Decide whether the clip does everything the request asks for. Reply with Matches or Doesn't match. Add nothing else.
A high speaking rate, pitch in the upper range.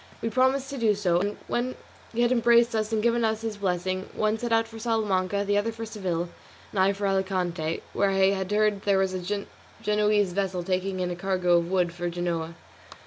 Matches